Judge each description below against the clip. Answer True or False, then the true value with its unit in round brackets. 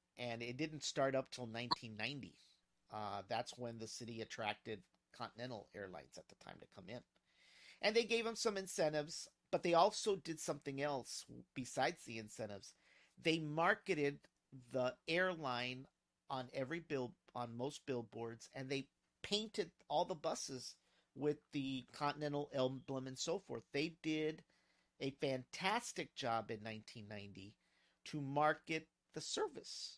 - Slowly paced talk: False (145 wpm)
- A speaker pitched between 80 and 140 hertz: True (135 Hz)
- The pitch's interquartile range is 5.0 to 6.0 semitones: True (5.3 semitones)